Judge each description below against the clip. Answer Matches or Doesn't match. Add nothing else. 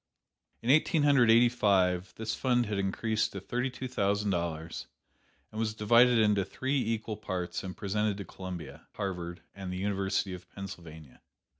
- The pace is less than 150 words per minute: Doesn't match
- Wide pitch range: Doesn't match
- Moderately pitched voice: Doesn't match